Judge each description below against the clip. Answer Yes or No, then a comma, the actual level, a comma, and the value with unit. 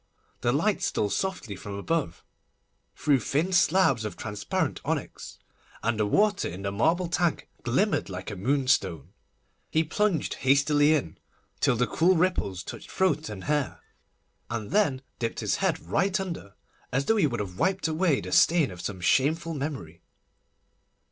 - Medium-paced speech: Yes, average, 155 wpm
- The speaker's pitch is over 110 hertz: Yes, medium, 140 Hz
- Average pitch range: No, wide, 8.8 semitones